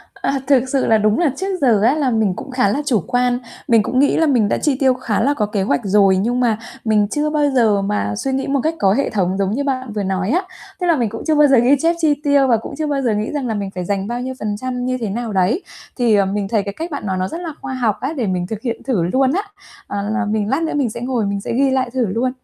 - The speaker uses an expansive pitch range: No, average, 4.8 semitones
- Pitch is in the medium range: No, high, 240 Hz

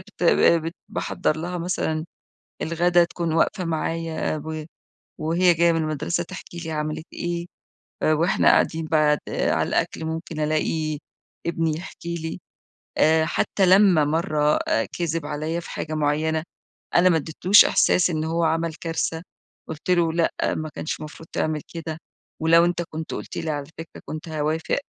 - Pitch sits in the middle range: Yes, medium, 160 Hz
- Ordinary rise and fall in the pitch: No, narrow, 1.6 semitones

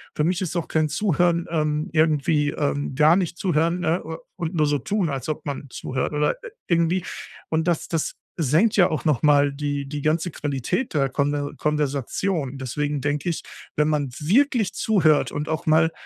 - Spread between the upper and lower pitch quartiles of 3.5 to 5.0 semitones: No, average, 2.7 semitones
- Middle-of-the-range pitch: Yes, medium, 155 Hz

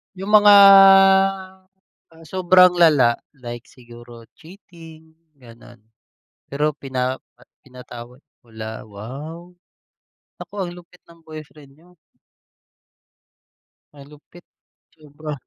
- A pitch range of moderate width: No, wide, 5.7 semitones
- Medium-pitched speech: Yes, medium, 150 Hz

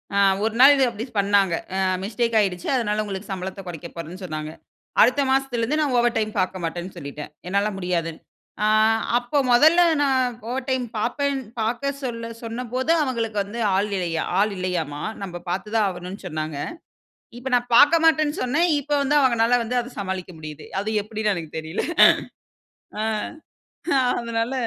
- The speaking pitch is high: Yes, high, 215 Hz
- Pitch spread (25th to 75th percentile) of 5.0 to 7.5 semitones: Yes, wide, 5.4 semitones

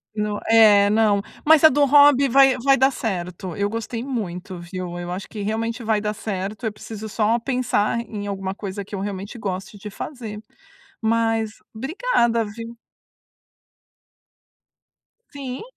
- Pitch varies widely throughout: No, average, 2.9 semitones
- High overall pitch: Yes, high, 220 Hz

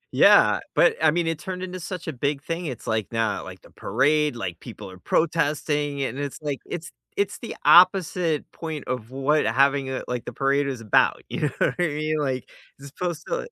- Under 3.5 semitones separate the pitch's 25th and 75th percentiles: No, average, 3.9 semitones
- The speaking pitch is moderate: Yes, medium, 145 Hz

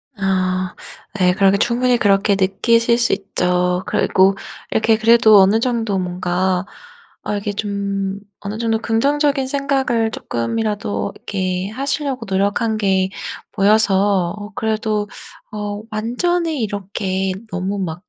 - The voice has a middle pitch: No, high, 205 Hz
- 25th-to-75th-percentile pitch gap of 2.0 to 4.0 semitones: Yes, average, 3.0 semitones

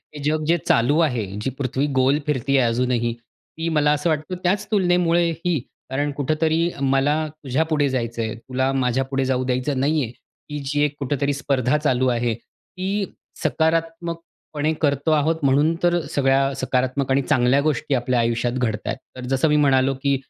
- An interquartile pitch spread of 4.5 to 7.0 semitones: No, average, 3.3 semitones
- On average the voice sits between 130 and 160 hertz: Yes, medium, 140 Hz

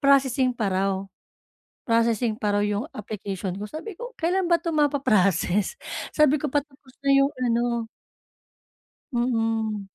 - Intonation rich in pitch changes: Yes, wide, 5.7 semitones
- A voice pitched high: Yes, high, 235 Hz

